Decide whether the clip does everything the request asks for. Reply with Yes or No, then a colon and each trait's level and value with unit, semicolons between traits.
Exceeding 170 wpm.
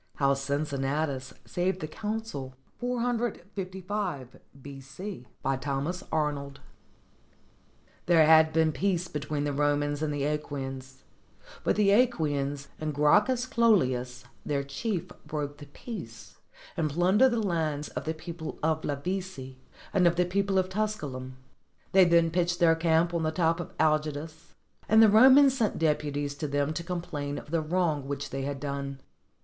No: average, 145 wpm